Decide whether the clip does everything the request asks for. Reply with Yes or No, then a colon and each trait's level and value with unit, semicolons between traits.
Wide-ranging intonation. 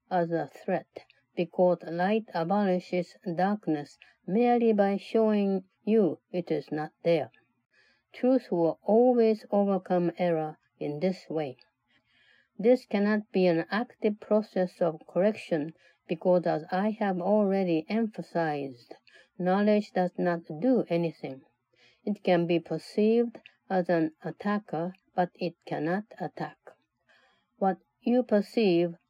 No: average, 3.8 semitones